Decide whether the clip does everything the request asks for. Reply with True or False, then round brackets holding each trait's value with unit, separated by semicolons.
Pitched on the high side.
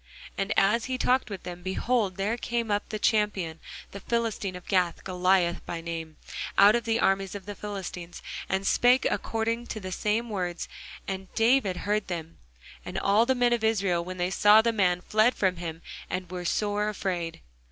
True (195 Hz)